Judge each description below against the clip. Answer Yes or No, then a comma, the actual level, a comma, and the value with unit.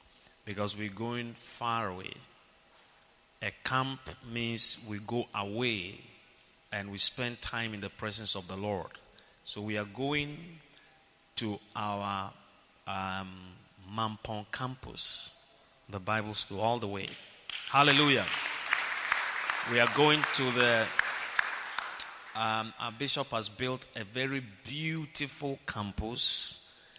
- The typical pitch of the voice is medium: No, low, 110 Hz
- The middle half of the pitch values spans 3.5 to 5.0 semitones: Yes, average, 3.9 semitones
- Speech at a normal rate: No, slow, 115 wpm